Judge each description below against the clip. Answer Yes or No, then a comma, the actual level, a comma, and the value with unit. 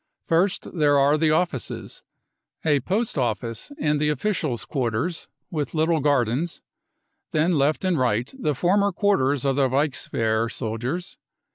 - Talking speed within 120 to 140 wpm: Yes, slow, 135 wpm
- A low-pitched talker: No, medium, 150 Hz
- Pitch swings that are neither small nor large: Yes, average, 4.9 semitones